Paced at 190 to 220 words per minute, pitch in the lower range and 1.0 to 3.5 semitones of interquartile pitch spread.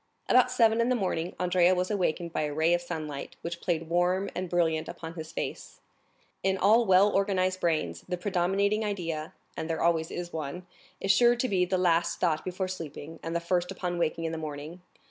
No: average, 195 wpm; medium, 175 Hz; average, 2.7 semitones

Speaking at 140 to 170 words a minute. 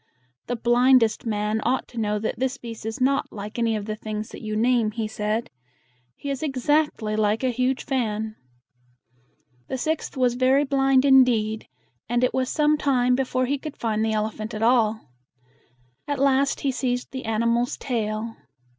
No: average, 180 wpm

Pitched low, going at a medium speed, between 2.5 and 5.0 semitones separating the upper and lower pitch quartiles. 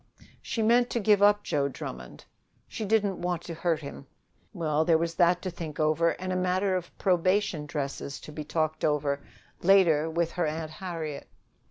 No: medium, 170 Hz; average, 180 wpm; average, 3.3 semitones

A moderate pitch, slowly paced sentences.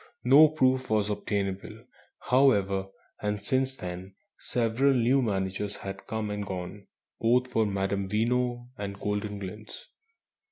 No: low, 105 Hz; slow, 120 wpm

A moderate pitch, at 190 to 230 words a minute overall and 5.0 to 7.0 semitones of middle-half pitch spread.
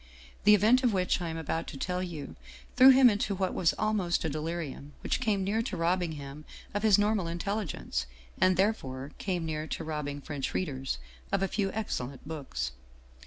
Yes: medium, 175 Hz; average, 200 wpm; average, 5.3 semitones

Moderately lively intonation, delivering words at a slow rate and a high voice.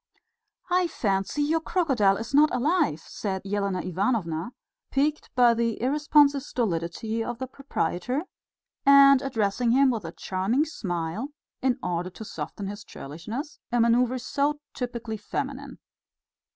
No: wide, 6.1 semitones; slow, 130 wpm; high, 235 Hz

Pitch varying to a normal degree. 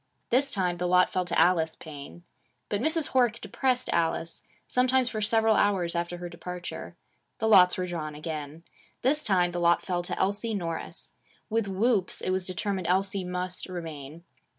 Yes: average, 3.8 semitones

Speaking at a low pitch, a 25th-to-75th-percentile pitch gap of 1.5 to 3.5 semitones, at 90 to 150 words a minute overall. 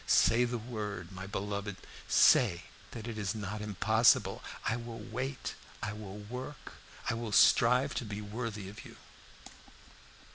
Yes: low, 110 Hz; narrow, 2.6 semitones; average, 145 wpm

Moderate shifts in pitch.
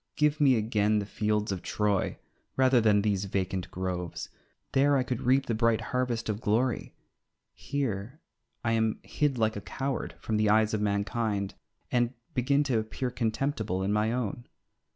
Yes: average, 3.5 semitones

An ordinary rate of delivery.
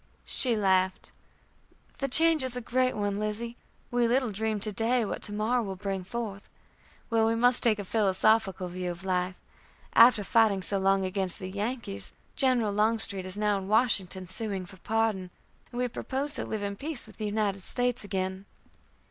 Yes: average, 180 wpm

